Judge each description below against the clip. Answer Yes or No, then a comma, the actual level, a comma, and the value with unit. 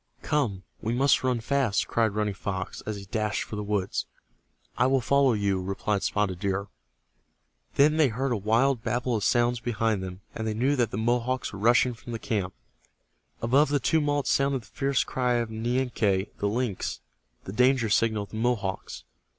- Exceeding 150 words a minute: Yes, average, 185 wpm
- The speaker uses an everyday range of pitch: Yes, average, 3.8 semitones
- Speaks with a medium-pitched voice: No, low, 115 Hz